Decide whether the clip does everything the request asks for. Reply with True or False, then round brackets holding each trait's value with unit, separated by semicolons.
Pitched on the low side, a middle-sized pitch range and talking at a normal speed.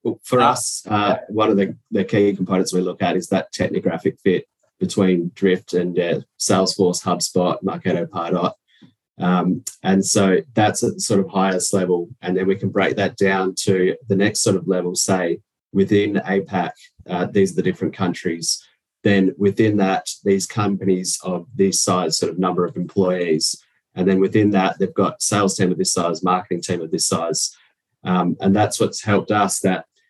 False (95 Hz; 1.4 semitones; 185 wpm)